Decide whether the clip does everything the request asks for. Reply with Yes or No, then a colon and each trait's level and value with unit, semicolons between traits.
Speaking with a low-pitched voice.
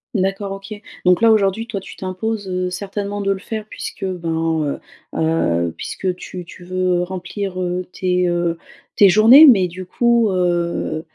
No: medium, 185 Hz